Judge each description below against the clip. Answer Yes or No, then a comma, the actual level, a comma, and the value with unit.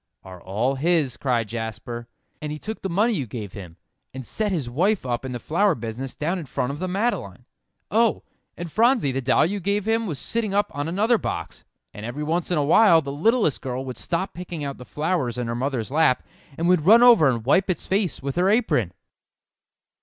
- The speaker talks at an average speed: No, fast, 215 wpm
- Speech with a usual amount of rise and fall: No, wide, 7.6 semitones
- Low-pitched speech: No, medium, 150 Hz